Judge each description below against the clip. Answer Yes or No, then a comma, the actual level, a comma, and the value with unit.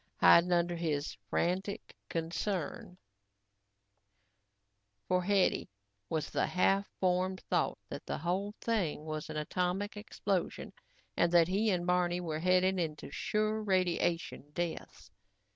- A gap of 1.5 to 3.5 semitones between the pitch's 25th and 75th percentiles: Yes, narrow, 2.4 semitones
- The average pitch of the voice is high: No, medium, 180 Hz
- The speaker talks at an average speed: No, slow, 120 wpm